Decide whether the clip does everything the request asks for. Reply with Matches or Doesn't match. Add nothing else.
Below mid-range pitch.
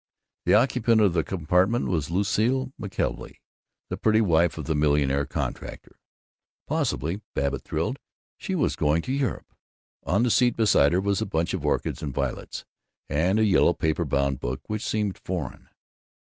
Matches